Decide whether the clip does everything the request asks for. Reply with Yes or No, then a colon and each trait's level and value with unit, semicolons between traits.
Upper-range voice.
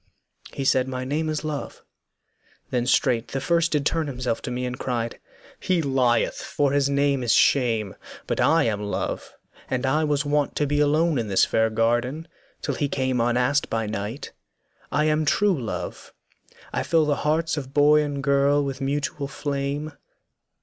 No: medium, 140 Hz